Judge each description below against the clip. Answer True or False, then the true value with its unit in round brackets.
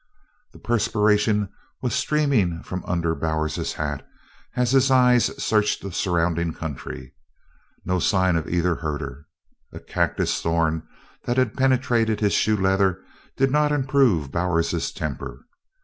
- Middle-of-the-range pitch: False (95 Hz)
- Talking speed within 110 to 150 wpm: True (135 wpm)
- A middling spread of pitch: False (6.6 semitones)